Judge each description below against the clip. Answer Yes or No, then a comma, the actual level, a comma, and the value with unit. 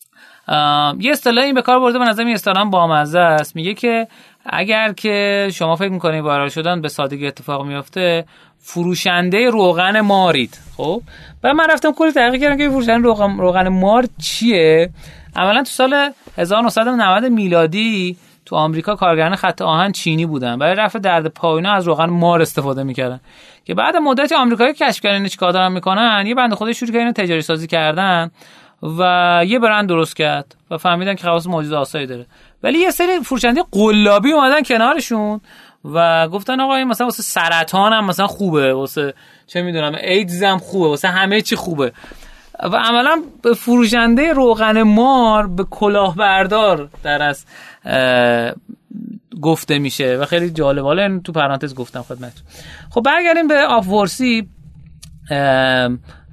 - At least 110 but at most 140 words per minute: No, average, 150 wpm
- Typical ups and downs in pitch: No, wide, 6.2 semitones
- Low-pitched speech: No, high, 190 Hz